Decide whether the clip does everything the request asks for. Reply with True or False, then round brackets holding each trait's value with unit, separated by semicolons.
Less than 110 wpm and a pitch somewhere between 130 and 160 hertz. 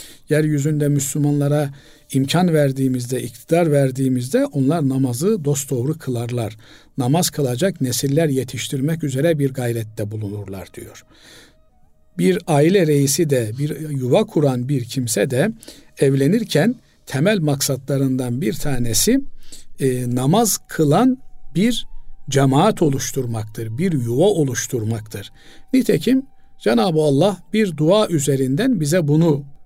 True (100 wpm; 140 Hz)